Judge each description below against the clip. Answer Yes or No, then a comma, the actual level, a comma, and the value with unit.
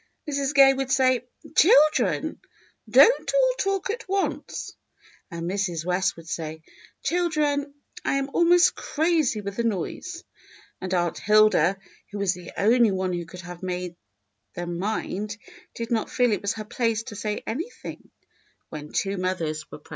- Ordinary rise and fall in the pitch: No, wide, 7.6 semitones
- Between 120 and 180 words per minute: Yes, average, 155 wpm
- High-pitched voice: Yes, high, 215 Hz